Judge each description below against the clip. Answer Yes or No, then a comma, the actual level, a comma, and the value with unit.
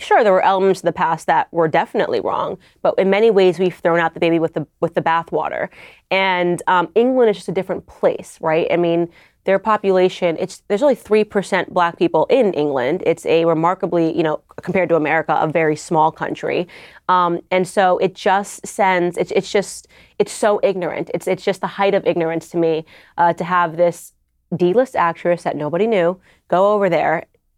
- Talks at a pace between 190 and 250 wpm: Yes, average, 195 wpm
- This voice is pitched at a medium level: Yes, medium, 180 Hz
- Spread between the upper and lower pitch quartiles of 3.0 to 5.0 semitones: No, narrow, 2.4 semitones